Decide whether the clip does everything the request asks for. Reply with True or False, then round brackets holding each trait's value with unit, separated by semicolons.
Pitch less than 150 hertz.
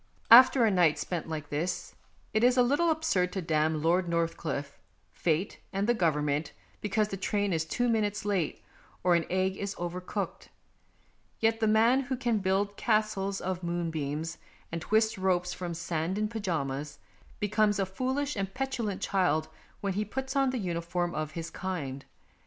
False (190 Hz)